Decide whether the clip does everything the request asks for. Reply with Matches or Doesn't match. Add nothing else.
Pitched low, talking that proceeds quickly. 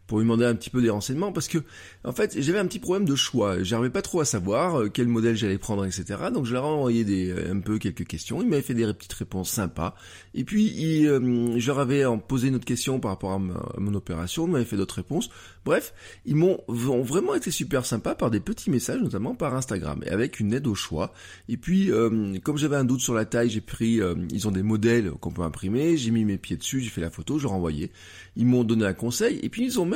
Matches